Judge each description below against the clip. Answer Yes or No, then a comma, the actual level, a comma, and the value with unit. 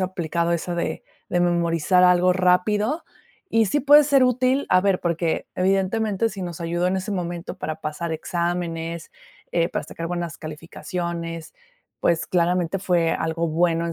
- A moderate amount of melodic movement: No, narrow, 2.0 semitones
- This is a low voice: No, medium, 175 Hz